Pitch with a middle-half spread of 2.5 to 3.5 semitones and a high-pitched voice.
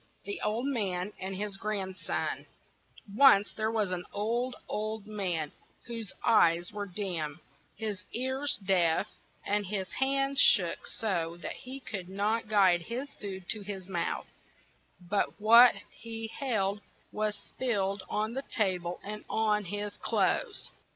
Yes: average, 3.2 semitones; high, 210 Hz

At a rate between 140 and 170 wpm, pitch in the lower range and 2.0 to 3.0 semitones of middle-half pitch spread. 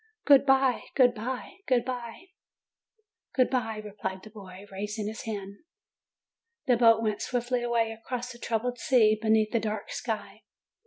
No: average, 155 wpm; high, 230 Hz; average, 2.7 semitones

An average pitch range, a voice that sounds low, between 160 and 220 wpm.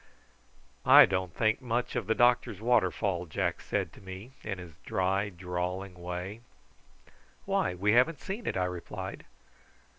No: average, 3.8 semitones; very low, 95 Hz; average, 145 wpm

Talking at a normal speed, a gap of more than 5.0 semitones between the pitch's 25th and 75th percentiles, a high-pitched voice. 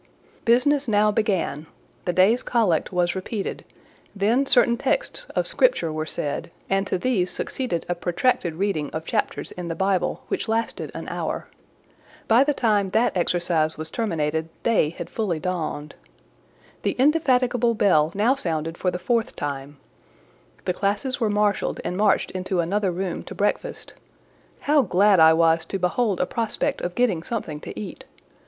Yes: average, 160 wpm; wide, 5.5 semitones; high, 195 Hz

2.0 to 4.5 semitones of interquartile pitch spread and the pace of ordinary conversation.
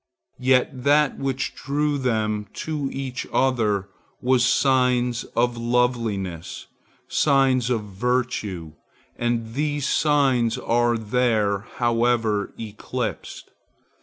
No: average, 2.9 semitones; slow, 95 wpm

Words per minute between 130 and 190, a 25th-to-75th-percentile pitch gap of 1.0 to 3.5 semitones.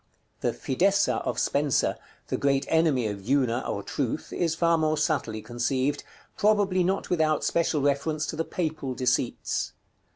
No: average, 150 wpm; average, 4.2 semitones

